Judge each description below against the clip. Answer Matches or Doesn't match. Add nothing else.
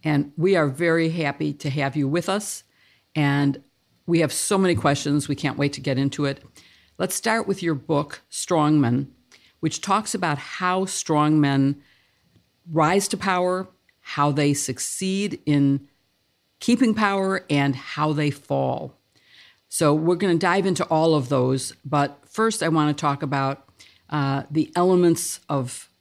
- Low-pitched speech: Doesn't match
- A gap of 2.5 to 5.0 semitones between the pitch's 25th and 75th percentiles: Matches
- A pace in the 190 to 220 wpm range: Doesn't match